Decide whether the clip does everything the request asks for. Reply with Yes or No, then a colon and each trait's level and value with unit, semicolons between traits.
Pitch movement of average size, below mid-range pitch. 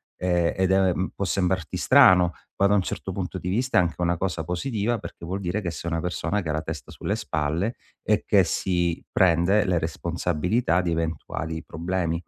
No: narrow, 2.3 semitones; very low, 90 Hz